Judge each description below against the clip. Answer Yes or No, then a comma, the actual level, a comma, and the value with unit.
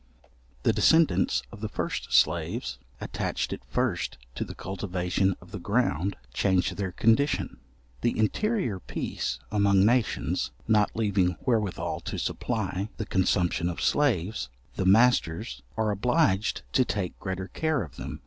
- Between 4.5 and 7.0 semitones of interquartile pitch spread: No, average, 3.8 semitones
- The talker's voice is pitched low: Yes, low, 100 Hz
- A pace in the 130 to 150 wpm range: Yes, average, 140 wpm